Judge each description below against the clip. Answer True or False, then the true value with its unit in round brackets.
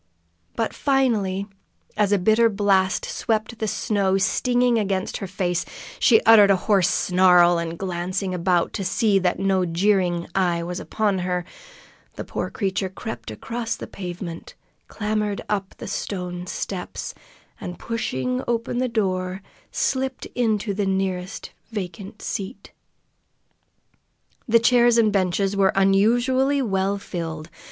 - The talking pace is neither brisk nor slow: False (130 wpm)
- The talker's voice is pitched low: False (195 Hz)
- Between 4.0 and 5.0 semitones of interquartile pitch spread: False (3.2 semitones)